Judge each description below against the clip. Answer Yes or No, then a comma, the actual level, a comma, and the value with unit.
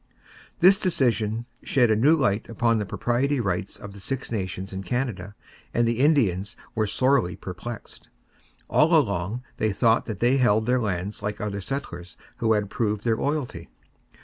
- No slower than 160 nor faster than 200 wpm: Yes, average, 165 wpm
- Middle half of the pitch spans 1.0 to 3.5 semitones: No, average, 3.9 semitones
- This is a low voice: Yes, low, 110 Hz